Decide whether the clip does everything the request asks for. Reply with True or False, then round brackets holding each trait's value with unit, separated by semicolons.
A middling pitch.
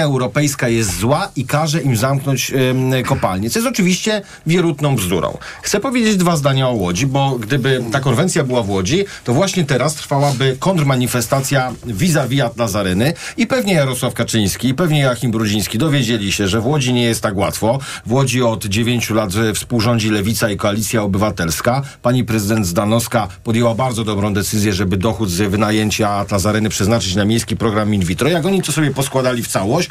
False (120 Hz)